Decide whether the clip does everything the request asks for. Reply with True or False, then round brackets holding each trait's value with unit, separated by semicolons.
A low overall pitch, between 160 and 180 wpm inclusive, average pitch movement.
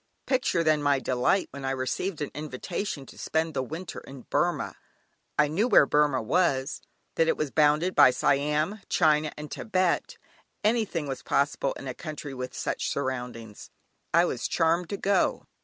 False (150 Hz; 165 wpm; 4.0 semitones)